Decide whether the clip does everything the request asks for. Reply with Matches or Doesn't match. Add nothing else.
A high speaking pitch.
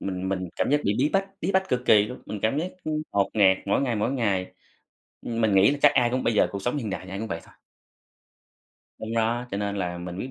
Doesn't match